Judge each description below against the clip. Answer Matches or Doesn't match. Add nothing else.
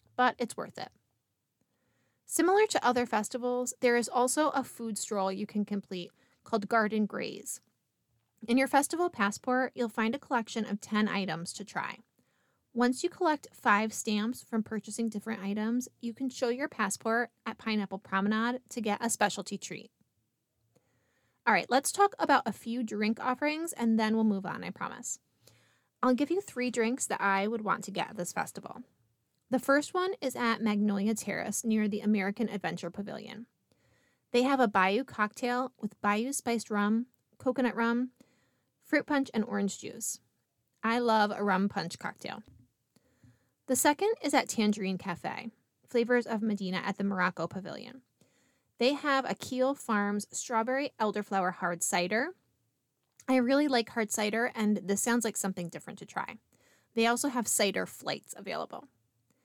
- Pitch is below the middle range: Doesn't match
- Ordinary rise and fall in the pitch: Matches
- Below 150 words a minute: Doesn't match